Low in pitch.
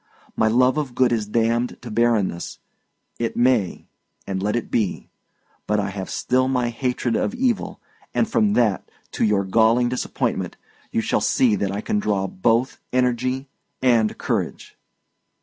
Yes: low, 115 Hz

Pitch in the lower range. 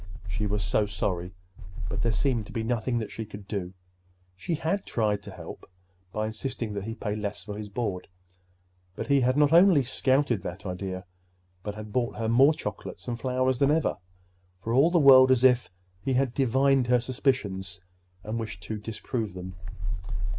Yes: low, 110 Hz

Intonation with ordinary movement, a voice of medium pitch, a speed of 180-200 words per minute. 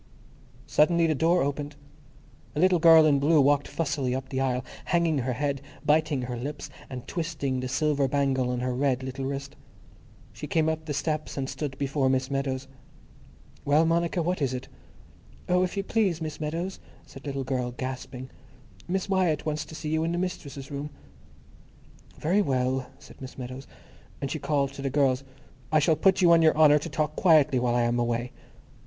Yes: average, 3.3 semitones; medium, 145 Hz; average, 190 wpm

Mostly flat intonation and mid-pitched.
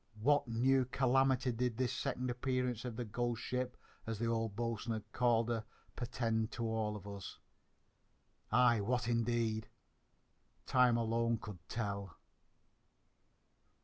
No: narrow, 2.0 semitones; low, 115 Hz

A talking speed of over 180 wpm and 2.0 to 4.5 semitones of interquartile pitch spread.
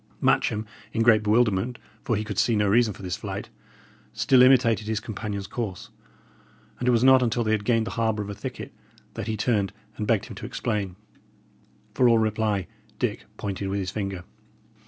Yes: average, 190 wpm; narrow, 2.4 semitones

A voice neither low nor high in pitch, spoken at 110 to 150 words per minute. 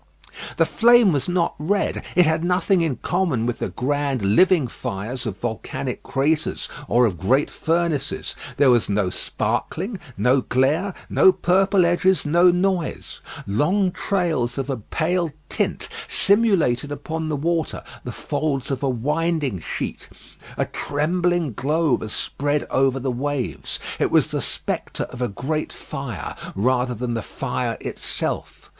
Yes: medium, 145 Hz; average, 145 wpm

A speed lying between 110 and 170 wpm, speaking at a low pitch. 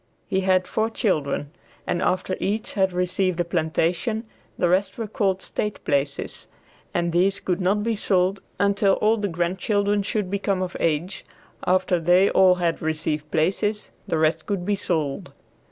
No: average, 160 wpm; medium, 185 Hz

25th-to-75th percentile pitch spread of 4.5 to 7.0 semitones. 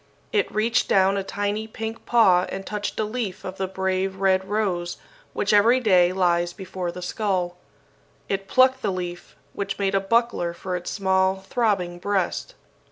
No: narrow, 2.5 semitones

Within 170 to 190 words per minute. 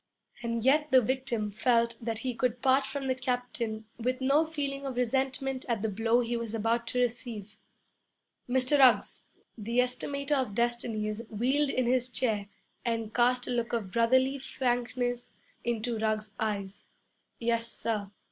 No: average, 155 wpm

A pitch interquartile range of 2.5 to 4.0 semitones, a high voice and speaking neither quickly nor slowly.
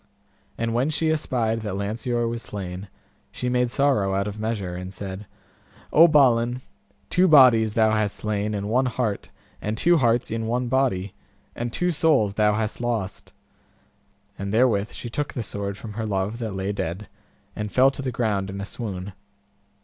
No: average, 3.6 semitones; low, 110 Hz; average, 175 wpm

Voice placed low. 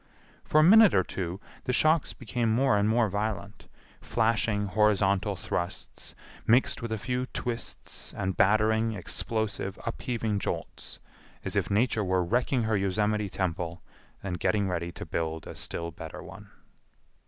Yes: low, 105 Hz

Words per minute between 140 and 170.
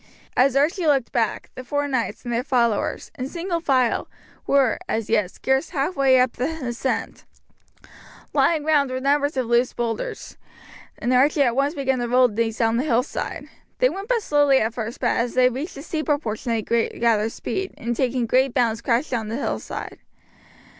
No: average, 180 wpm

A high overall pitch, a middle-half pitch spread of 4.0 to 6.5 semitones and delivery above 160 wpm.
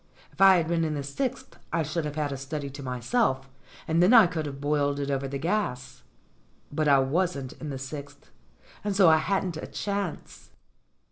No: medium, 150 Hz; average, 4.3 semitones; average, 200 wpm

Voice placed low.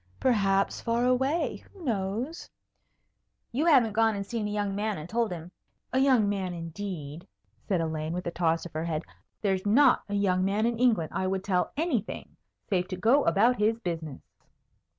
No: high, 205 Hz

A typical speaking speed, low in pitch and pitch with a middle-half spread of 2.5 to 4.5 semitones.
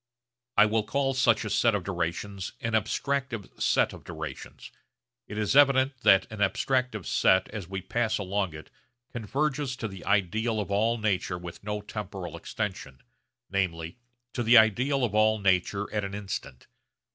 Yes: average, 160 wpm; low, 105 Hz; average, 3.4 semitones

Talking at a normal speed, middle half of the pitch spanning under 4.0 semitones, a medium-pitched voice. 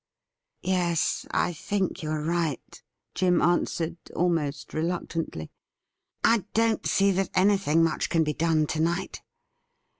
Yes: average, 145 wpm; average, 2.8 semitones; medium, 170 Hz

